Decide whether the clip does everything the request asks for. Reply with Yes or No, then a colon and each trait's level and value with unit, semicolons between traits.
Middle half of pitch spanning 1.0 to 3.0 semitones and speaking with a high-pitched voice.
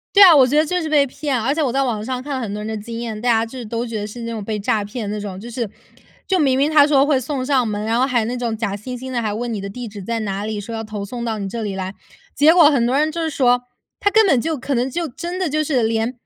No: average, 4.4 semitones; high, 240 Hz